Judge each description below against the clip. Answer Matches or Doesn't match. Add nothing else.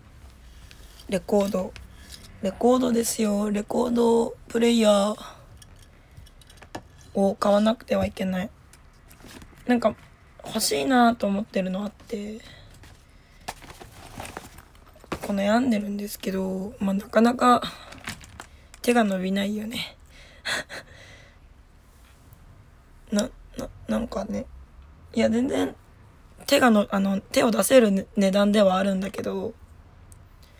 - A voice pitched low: Doesn't match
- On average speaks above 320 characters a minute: Doesn't match